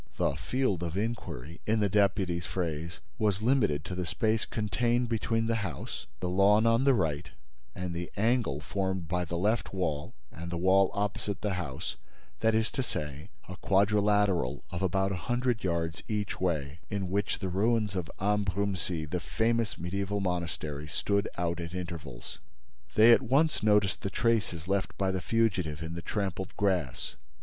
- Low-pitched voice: Yes, very low, 95 Hz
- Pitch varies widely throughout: No, average, 3.8 semitones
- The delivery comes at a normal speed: Yes, average, 170 wpm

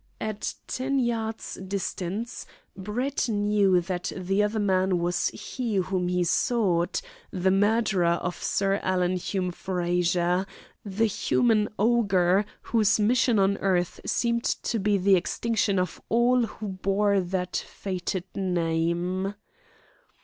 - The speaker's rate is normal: No, slow, 120 wpm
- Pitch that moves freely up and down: No, average, 3.1 semitones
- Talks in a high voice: Yes, high, 195 Hz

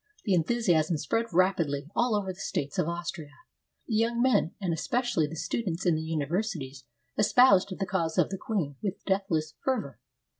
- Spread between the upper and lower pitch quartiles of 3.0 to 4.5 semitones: No, average, 5.2 semitones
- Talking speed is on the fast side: No, average, 175 wpm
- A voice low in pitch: No, medium, 185 Hz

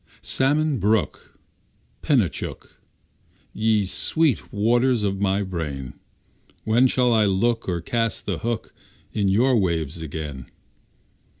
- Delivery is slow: Yes, slow, 110 wpm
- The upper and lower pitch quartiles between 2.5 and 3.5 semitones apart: No, average, 4.5 semitones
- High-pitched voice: No, low, 105 Hz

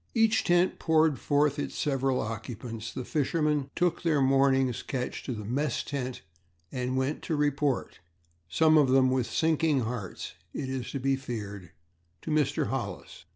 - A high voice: No, low, 135 Hz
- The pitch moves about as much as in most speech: Yes, average, 3.2 semitones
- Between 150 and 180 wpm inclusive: Yes, average, 160 wpm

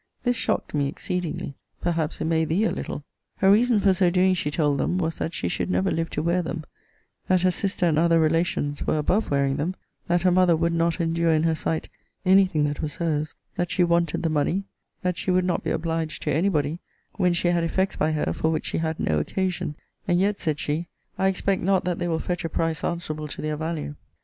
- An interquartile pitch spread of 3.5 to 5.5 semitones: No, average, 2.8 semitones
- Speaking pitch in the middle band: Yes, medium, 170 Hz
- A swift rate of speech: Yes, fast, 235 wpm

